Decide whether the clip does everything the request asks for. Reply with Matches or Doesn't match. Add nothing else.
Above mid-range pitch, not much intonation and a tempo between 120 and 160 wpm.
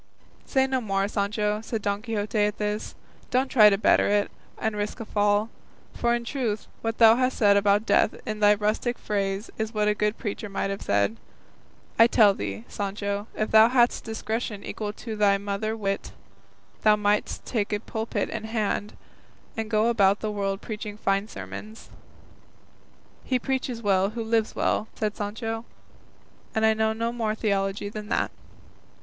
Doesn't match